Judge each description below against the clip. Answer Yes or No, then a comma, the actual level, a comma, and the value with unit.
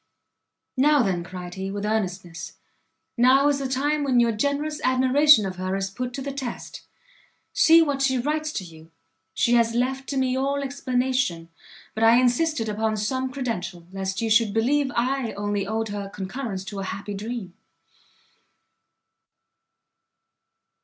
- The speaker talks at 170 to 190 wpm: No, average, 155 wpm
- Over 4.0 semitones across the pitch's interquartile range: Yes, average, 5.3 semitones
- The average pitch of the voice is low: No, high, 235 Hz